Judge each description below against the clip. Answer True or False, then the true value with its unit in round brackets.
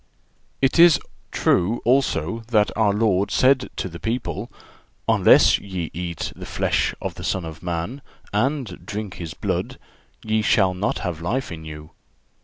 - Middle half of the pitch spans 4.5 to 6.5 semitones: True (5.3 semitones)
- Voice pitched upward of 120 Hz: False (100 Hz)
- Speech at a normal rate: True (155 wpm)